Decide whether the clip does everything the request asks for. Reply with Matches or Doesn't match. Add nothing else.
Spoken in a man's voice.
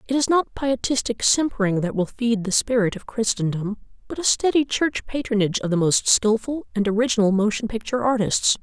Doesn't match